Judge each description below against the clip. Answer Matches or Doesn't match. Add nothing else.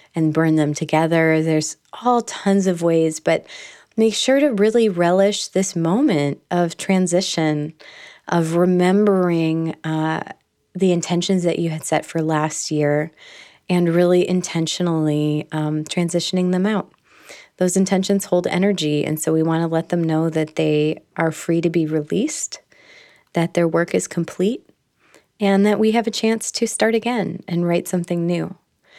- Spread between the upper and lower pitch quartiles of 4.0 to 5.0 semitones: Doesn't match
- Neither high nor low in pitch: Matches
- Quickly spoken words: Doesn't match